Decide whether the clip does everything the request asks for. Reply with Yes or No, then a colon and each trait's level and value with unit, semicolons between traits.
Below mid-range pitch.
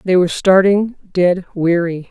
No: medium, 180 Hz